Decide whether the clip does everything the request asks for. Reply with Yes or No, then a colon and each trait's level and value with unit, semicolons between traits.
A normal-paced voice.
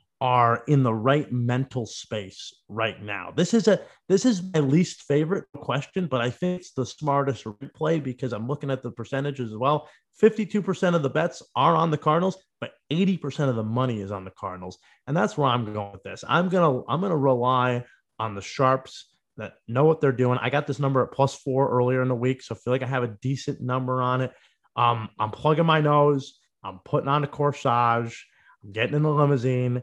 No: fast, 215 wpm